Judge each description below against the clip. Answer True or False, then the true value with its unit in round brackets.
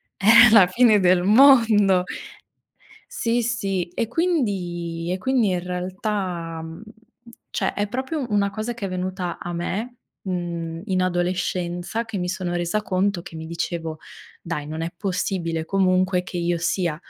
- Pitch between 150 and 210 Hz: True (185 Hz)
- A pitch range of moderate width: True (3.6 semitones)